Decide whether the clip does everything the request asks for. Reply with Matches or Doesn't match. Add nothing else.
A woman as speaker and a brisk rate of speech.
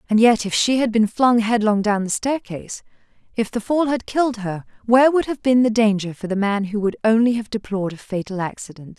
Matches